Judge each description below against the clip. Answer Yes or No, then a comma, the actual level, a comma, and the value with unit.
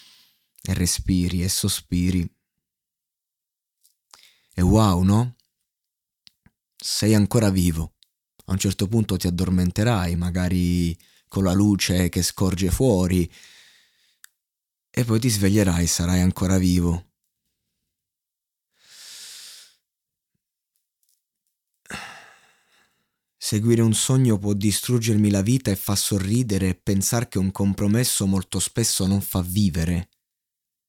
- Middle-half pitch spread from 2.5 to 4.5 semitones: Yes, average, 2.8 semitones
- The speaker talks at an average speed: No, slow, 100 wpm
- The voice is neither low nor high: No, very low, 95 Hz